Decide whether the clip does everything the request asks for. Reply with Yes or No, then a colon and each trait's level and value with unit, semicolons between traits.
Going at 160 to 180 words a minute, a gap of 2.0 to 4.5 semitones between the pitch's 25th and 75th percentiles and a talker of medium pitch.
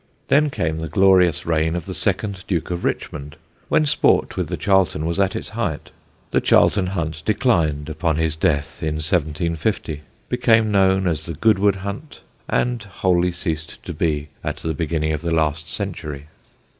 No: average, 170 wpm; average, 3.8 semitones; very low, 85 Hz